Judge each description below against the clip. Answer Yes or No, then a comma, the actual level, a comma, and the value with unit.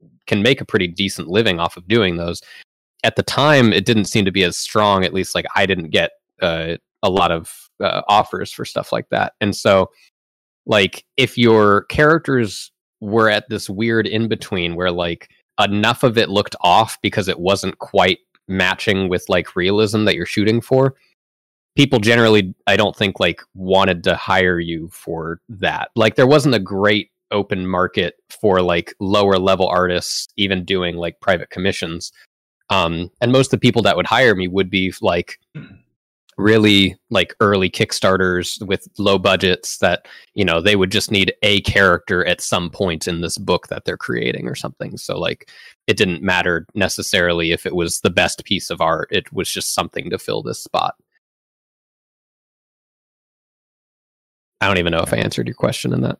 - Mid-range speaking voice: No, very low, 95 Hz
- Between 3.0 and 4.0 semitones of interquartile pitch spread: Yes, average, 3.3 semitones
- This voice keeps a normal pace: Yes, average, 180 wpm